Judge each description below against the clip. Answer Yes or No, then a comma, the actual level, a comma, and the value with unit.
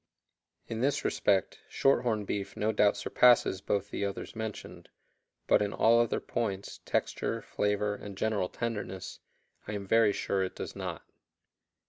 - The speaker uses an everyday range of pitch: No, narrow, 2.2 semitones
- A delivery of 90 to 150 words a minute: Yes, average, 145 wpm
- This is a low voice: Yes, low, 105 Hz